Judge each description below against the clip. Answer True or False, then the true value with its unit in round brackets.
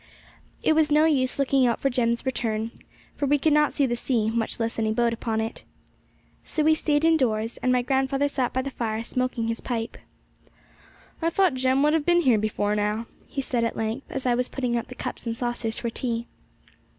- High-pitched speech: True (250 Hz)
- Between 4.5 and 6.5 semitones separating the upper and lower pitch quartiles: False (3.3 semitones)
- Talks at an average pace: False (210 wpm)